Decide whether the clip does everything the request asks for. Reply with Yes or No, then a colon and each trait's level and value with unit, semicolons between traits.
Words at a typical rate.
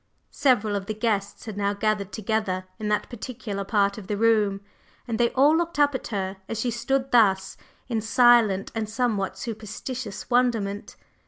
Yes: average, 170 wpm